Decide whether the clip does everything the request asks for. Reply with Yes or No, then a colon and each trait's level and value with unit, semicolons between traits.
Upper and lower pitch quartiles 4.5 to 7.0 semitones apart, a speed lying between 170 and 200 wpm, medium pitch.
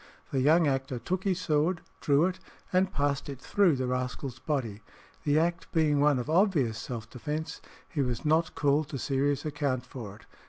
No: average, 3.6 semitones; average, 185 wpm; medium, 145 Hz